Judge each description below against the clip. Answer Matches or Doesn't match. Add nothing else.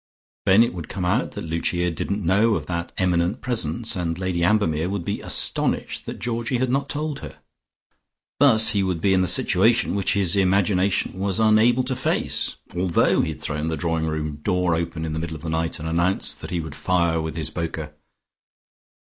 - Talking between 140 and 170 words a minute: Doesn't match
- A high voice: Doesn't match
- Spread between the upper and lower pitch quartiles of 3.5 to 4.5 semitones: Matches